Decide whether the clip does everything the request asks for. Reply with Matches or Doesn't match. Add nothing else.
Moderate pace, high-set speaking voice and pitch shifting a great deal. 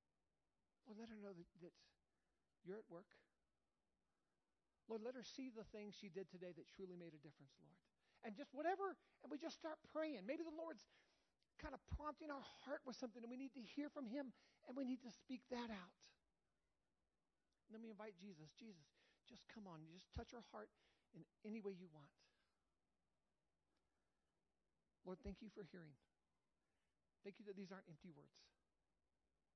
Matches